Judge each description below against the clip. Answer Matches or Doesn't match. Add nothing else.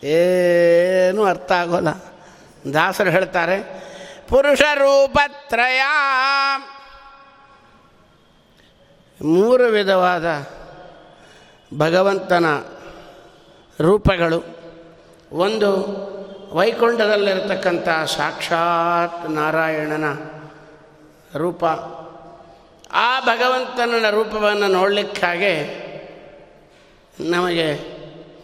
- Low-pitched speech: Doesn't match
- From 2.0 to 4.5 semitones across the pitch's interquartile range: Doesn't match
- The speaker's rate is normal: Doesn't match